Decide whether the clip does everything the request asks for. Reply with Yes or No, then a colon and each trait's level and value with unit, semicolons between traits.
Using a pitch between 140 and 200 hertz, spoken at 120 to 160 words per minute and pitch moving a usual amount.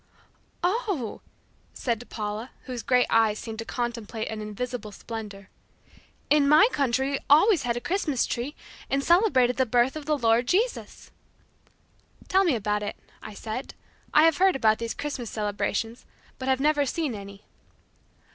No: very high, 250 Hz; average, 155 wpm; average, 4.9 semitones